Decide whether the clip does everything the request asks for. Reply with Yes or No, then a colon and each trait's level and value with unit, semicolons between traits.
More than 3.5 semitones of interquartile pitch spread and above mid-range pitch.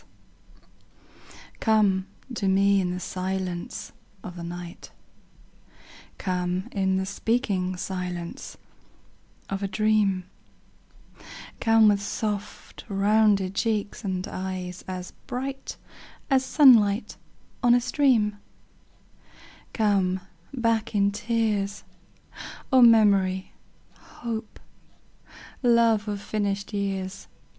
No: average, 2.8 semitones; high, 200 Hz